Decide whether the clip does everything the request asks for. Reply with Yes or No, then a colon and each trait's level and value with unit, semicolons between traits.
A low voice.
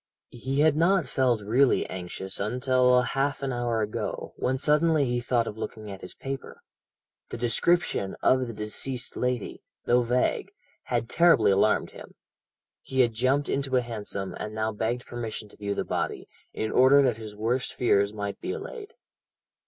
Yes: low, 120 Hz